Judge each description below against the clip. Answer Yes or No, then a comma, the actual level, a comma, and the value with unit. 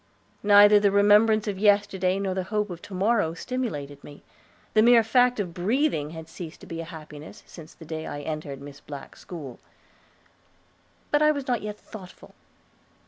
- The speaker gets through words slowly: No, average, 175 wpm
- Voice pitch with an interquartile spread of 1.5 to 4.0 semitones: No, average, 5.2 semitones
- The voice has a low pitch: No, high, 190 Hz